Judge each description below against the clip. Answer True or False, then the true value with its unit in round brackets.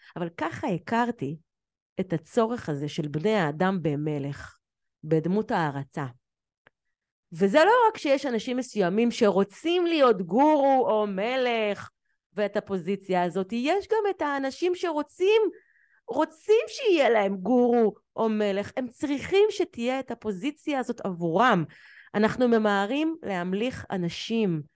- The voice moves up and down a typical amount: False (6.6 semitones)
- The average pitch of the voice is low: False (220 Hz)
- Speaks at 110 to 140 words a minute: True (115 wpm)